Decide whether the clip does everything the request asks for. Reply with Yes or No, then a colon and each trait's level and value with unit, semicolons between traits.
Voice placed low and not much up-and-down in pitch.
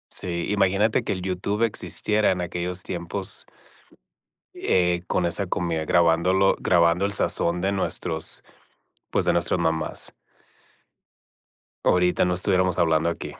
Yes: very low, 90 Hz; narrow, 2.1 semitones